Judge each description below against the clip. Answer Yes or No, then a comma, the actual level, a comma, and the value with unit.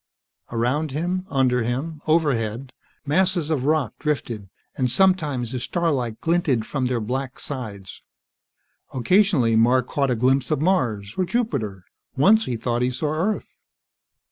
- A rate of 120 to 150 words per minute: Yes, average, 140 wpm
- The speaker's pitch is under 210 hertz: Yes, low, 135 Hz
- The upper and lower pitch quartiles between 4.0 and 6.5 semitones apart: Yes, average, 5.1 semitones